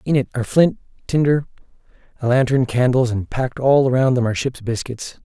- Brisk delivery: No, average, 180 wpm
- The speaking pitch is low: Yes, low, 130 Hz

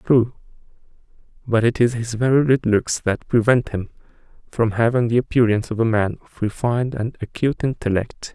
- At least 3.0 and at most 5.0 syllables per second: No, 5.4 syllables/s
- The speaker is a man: Yes, male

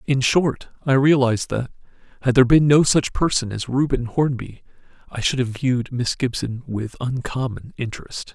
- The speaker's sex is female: No, male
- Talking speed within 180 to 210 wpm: No, average, 165 wpm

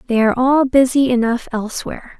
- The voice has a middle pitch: No, very high, 250 Hz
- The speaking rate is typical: Yes, average, 165 wpm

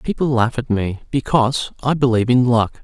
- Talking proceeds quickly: No, average, 190 wpm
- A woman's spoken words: No, male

